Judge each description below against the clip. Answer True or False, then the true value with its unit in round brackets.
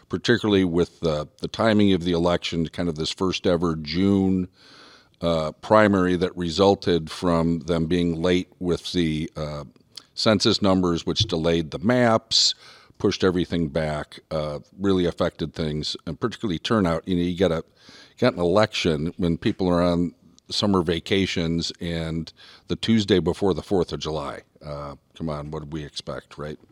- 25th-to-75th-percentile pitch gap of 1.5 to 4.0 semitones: True (2.8 semitones)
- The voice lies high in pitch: False (85 Hz)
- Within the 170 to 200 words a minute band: False (155 wpm)